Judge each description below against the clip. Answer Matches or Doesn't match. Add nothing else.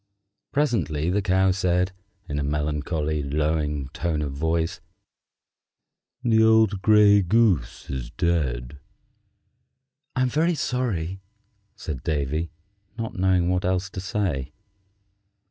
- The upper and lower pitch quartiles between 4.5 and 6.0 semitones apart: Matches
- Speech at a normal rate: Doesn't match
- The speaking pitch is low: Matches